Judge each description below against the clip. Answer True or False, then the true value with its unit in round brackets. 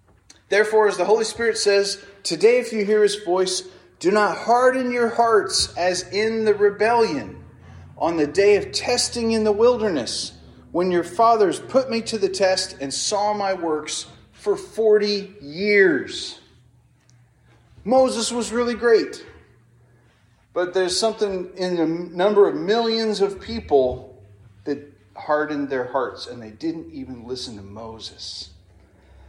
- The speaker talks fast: False (140 wpm)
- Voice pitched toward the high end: True (195 Hz)